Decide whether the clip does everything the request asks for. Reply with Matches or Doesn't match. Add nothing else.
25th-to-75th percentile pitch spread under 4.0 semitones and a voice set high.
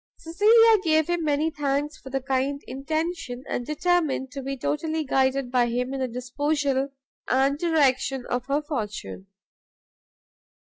Matches